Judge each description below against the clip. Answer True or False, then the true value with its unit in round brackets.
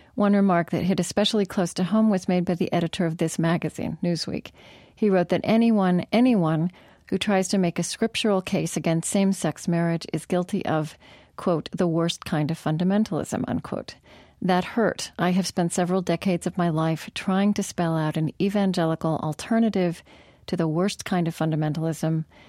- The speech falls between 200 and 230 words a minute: False (175 wpm)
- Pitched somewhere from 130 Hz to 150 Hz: False (180 Hz)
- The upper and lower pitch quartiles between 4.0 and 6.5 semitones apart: False (3.0 semitones)